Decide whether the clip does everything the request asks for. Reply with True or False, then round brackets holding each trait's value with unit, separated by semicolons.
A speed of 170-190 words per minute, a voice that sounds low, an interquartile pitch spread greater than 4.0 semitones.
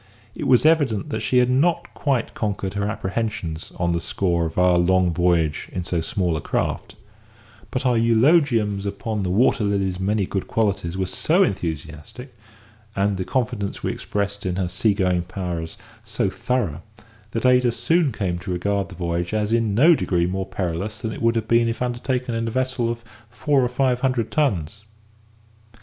True (180 wpm; 105 Hz; 5.2 semitones)